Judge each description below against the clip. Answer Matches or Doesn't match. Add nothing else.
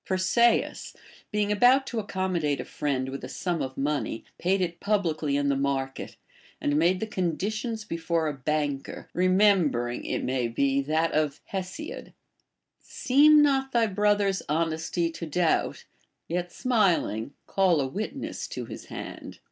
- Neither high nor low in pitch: Matches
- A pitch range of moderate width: Doesn't match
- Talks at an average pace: Matches